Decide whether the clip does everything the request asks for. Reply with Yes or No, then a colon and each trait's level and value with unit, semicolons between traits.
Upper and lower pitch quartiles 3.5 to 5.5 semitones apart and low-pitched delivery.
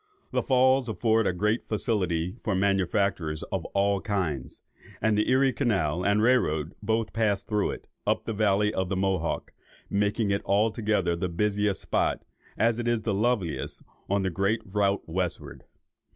No: average, 2.8 semitones; low, 100 Hz